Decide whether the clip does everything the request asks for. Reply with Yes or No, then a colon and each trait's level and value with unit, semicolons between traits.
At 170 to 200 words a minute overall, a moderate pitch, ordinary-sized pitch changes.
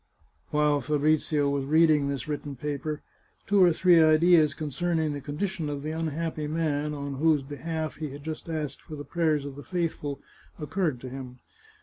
No: average, 180 wpm; medium, 150 Hz; narrow, 2.0 semitones